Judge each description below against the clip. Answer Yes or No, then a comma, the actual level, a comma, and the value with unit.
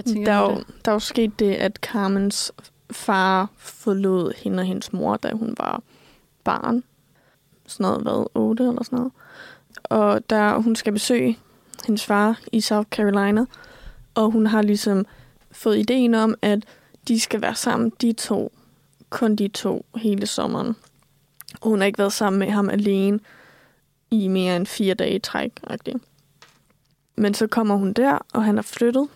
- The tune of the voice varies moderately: No, narrow, 2.3 semitones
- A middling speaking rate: Yes, average, 160 wpm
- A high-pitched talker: Yes, high, 215 Hz